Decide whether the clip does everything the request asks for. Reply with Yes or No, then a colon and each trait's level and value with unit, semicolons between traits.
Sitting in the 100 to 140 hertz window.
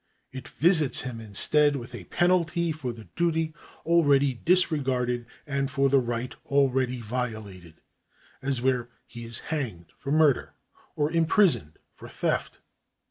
Yes: low, 135 Hz